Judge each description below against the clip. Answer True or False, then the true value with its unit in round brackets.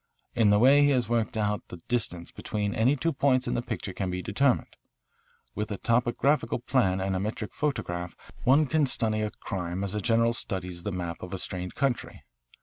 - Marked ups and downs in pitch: False (4.9 semitones)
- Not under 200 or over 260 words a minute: True (205 wpm)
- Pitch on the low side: True (110 Hz)